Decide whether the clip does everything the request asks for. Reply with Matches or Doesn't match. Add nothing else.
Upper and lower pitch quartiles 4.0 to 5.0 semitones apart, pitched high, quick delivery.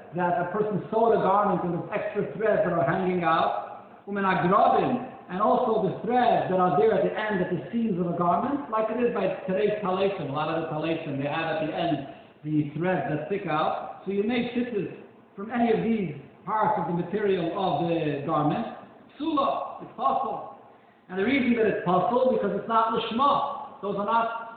Matches